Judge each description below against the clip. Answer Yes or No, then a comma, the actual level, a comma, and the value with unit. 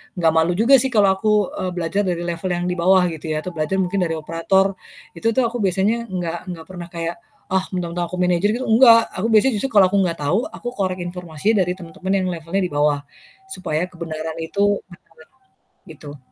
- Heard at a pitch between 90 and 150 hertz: No, medium, 180 Hz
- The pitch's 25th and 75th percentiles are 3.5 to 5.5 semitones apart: No, average, 3.0 semitones